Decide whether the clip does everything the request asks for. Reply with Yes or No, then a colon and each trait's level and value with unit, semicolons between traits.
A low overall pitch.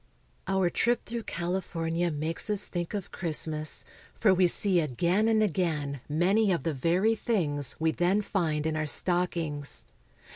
No: medium, 175 Hz